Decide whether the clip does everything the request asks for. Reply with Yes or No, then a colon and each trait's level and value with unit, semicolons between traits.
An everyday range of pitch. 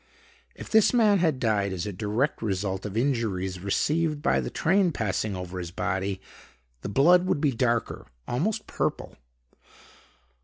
No: wide, 8.4 semitones